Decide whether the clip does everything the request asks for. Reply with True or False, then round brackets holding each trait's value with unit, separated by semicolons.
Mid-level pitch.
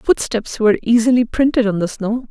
False (230 Hz)